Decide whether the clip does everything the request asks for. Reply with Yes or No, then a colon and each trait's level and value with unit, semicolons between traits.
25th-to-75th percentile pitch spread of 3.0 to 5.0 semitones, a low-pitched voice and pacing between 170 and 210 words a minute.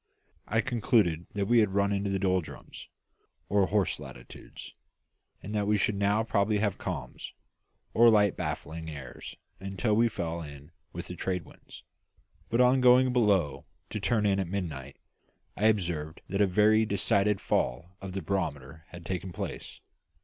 No: average, 3.8 semitones; low, 100 Hz; average, 160 wpm